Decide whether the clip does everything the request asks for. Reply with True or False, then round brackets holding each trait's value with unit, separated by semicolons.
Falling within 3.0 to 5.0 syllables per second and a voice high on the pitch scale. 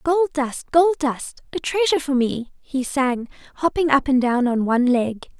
True (4.9 syllables/s; 275 Hz)